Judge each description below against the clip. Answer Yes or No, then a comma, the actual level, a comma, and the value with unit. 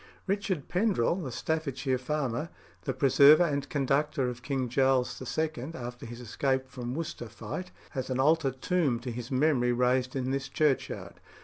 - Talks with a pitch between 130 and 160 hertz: Yes, low, 135 Hz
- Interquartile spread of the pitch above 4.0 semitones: No, average, 3.6 semitones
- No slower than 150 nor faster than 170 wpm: Yes, average, 155 wpm